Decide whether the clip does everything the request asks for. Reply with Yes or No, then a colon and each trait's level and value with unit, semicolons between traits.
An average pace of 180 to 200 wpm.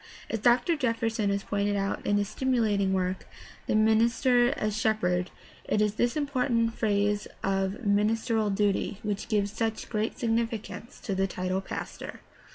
No: average, 155 wpm